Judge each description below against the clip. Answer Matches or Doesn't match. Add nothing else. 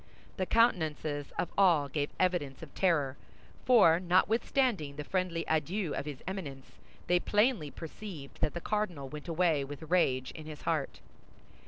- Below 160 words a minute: Matches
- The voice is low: Doesn't match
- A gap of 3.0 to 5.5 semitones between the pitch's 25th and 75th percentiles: Matches